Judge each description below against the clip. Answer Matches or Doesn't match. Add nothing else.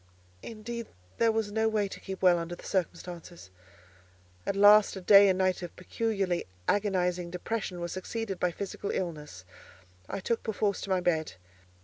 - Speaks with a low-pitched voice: Doesn't match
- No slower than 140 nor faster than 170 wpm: Matches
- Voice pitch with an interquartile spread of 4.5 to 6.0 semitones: Doesn't match